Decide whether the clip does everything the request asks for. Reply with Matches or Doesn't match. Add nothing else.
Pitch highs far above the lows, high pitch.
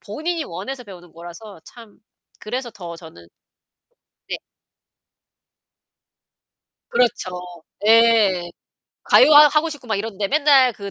Matches